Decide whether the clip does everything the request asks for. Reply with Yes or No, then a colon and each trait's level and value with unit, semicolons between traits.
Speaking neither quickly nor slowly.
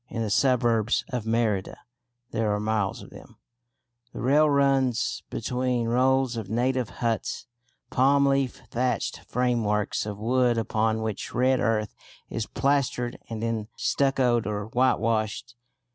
No: slow, 130 wpm